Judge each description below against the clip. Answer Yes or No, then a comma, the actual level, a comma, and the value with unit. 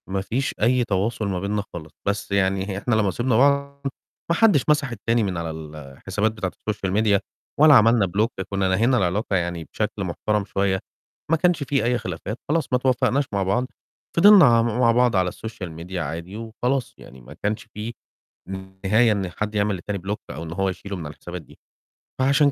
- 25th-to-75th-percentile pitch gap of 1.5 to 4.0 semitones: No, average, 4.6 semitones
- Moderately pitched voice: No, low, 105 Hz